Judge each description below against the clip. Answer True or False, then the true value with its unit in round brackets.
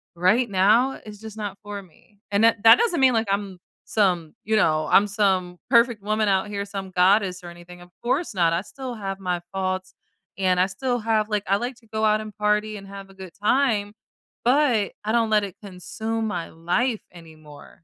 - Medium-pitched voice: False (205 Hz)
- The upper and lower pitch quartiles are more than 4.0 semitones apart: False (3.0 semitones)